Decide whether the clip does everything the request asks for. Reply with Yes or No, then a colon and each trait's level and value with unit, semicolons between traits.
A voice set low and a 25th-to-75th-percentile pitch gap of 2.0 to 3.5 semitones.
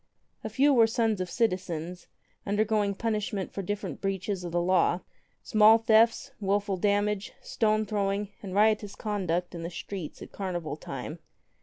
No: high, 200 Hz; average, 2.9 semitones